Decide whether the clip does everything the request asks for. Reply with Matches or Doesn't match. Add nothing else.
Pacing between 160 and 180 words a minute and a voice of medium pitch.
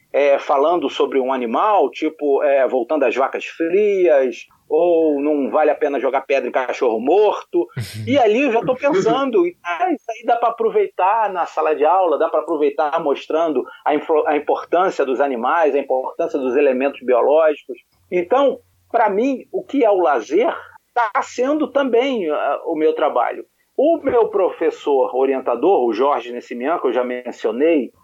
Doesn't match